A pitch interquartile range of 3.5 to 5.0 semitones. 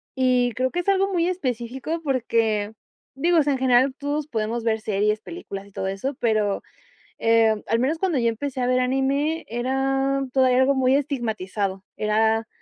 Yes: average, 3.8 semitones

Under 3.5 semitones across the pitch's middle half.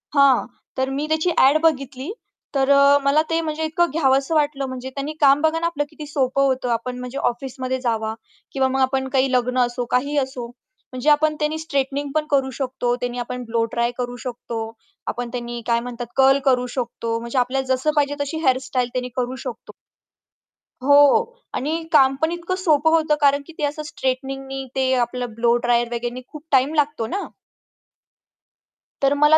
Yes: average, 2.9 semitones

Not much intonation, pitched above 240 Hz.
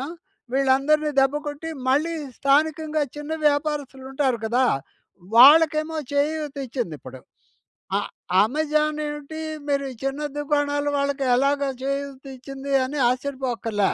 Yes: narrow, 1.9 semitones; very high, 280 Hz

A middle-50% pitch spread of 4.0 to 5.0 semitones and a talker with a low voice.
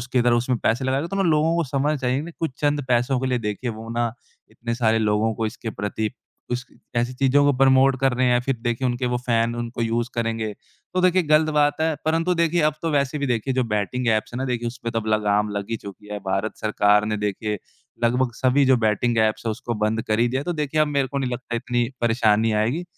No: average, 3.6 semitones; low, 120 Hz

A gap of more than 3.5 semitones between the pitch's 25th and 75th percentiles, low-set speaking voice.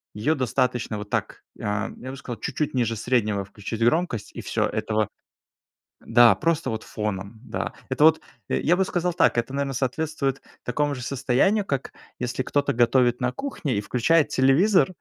Yes: average, 4.5 semitones; low, 125 Hz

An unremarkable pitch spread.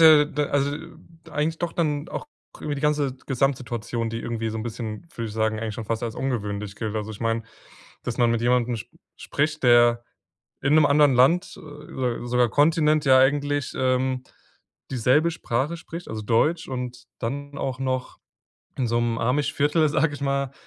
Yes: average, 3.8 semitones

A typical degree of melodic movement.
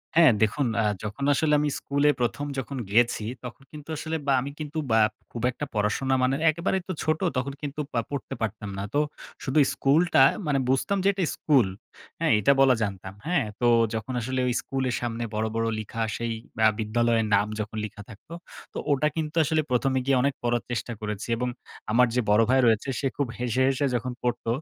Yes: average, 4.0 semitones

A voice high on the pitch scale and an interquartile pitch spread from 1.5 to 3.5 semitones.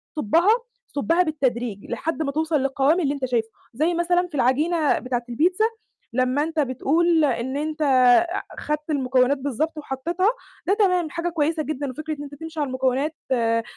No: very high, 295 Hz; average, 4.0 semitones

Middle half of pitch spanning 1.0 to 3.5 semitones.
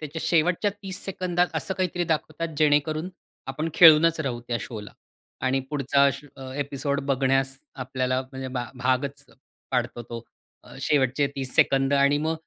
Yes: average, 3.2 semitones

